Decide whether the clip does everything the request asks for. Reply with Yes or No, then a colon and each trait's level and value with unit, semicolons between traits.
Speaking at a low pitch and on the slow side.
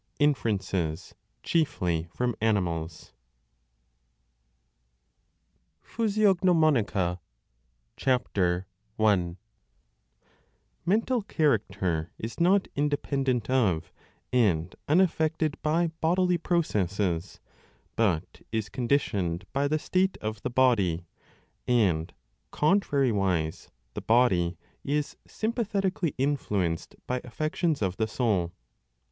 Yes: low, 120 Hz; slow, 80 wpm